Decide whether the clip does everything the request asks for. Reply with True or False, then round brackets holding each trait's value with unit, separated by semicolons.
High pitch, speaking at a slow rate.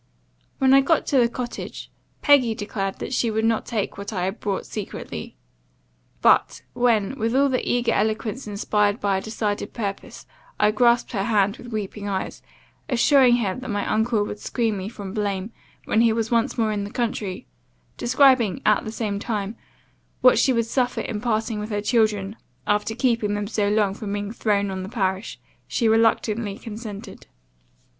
False (220 Hz; 180 wpm)